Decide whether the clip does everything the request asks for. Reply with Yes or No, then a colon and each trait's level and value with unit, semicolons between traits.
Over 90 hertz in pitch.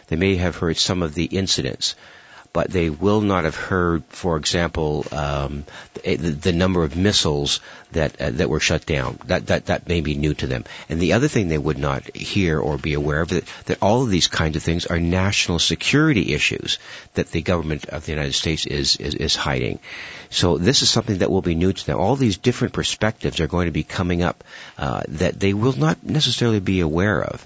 No: very low, 85 Hz